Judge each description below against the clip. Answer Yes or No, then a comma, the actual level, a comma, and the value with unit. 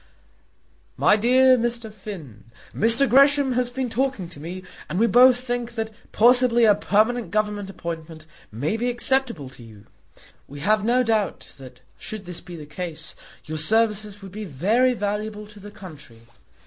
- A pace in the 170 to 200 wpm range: No, average, 160 wpm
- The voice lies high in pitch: Yes, high, 210 Hz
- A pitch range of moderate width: No, wide, 5.8 semitones